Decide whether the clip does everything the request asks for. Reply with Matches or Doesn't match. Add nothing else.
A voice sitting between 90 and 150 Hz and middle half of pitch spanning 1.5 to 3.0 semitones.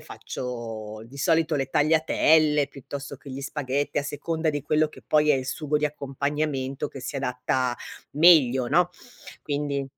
Matches